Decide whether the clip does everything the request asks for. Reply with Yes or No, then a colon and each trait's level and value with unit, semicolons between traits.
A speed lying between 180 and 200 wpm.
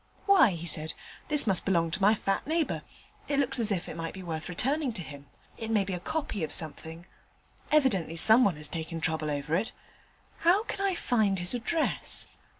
Yes: average, 195 wpm